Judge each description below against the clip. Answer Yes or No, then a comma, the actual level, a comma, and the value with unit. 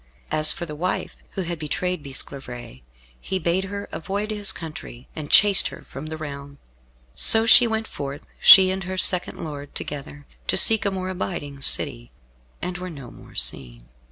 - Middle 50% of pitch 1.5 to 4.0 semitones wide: No, average, 5.0 semitones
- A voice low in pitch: No, medium, 160 Hz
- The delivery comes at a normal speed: Yes, average, 175 wpm